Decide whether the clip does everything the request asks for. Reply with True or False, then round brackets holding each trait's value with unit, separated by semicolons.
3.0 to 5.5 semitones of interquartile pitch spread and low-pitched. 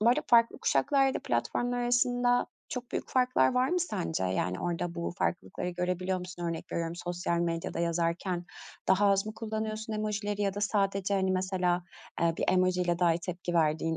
False (4.1 semitones; 185 Hz)